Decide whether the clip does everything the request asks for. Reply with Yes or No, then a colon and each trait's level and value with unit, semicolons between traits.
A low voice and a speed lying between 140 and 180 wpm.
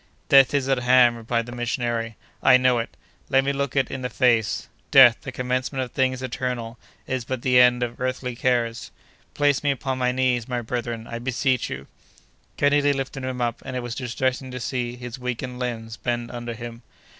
No: low, 125 Hz; average, 195 wpm